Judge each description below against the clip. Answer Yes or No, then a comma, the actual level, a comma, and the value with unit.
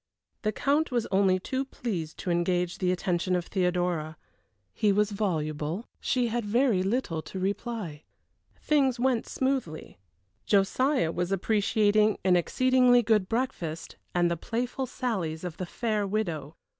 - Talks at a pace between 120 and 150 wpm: Yes, average, 140 wpm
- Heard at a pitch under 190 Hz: No, high, 200 Hz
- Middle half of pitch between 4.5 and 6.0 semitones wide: Yes, wide, 5.4 semitones